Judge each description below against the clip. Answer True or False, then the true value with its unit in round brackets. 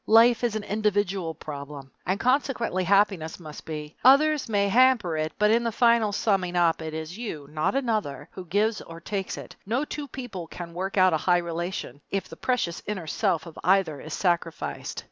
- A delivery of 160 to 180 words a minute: False (190 wpm)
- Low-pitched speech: False (190 Hz)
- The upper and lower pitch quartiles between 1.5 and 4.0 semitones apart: False (5.2 semitones)